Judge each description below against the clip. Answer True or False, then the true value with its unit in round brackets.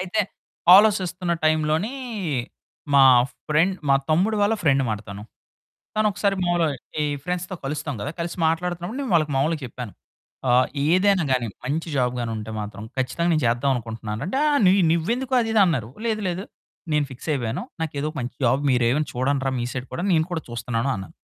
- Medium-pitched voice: True (155 Hz)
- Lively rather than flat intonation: True (6.1 semitones)